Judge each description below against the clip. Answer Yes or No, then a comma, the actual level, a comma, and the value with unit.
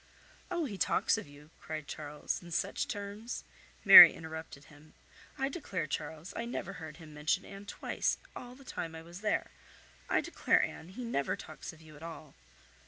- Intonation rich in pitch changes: No, average, 4.8 semitones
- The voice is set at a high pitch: No, medium, 165 Hz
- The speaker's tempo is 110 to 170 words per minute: No, average, 180 wpm